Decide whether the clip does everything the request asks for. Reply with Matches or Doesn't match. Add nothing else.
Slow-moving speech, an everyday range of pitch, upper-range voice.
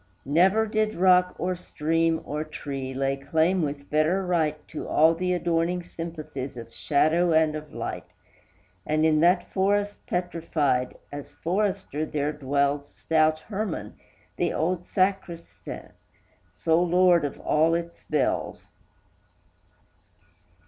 Doesn't match